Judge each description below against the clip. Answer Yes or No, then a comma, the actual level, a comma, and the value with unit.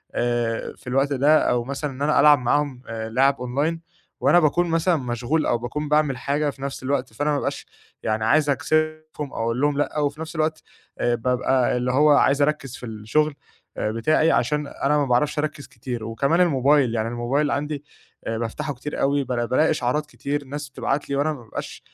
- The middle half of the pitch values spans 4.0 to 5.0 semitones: No, average, 3.4 semitones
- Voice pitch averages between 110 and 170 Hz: Yes, medium, 140 Hz